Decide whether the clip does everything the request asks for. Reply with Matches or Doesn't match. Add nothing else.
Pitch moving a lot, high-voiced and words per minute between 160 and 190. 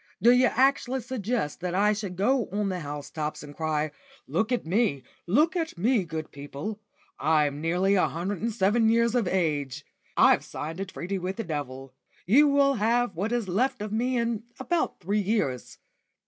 Matches